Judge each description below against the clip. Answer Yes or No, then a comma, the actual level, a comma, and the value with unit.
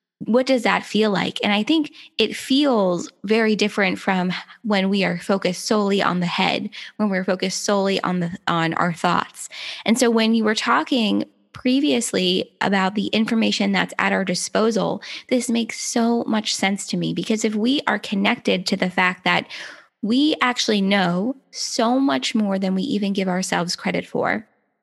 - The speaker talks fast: No, average, 175 wpm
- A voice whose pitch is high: Yes, high, 210 Hz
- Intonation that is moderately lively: Yes, average, 3.6 semitones